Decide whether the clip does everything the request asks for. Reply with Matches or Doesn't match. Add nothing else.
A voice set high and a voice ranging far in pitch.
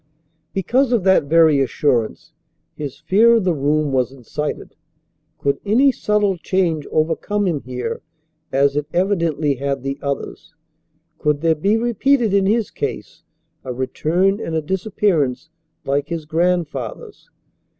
Doesn't match